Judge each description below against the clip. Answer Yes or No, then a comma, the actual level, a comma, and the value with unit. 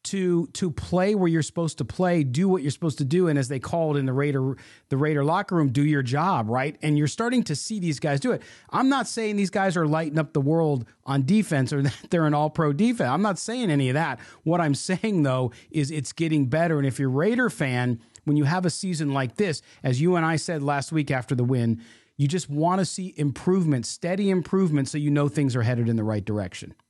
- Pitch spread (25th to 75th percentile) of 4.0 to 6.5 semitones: Yes, average, 4.5 semitones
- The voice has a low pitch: No, medium, 150 Hz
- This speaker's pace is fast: Yes, fast, 250 wpm